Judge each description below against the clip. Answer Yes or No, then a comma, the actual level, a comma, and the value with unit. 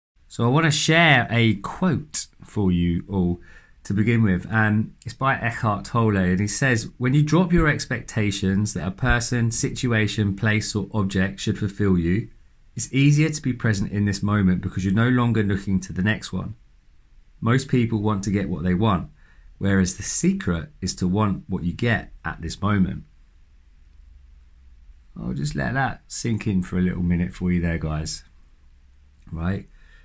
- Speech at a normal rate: Yes, average, 175 wpm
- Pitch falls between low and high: No, low, 100 Hz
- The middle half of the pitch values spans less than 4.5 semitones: No, average, 5.1 semitones